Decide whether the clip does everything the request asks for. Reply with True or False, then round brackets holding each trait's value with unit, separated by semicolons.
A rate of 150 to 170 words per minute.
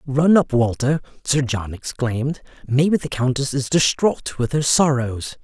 True (155 wpm)